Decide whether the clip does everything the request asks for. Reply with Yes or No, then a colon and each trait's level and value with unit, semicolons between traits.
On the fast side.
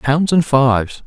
No: average, 170 wpm